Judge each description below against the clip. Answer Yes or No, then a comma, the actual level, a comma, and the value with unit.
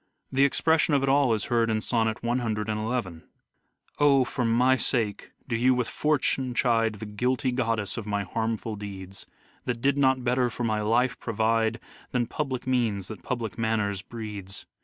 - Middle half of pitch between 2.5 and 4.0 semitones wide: Yes, average, 2.9 semitones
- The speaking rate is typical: Yes, average, 170 wpm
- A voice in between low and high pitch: No, low, 115 Hz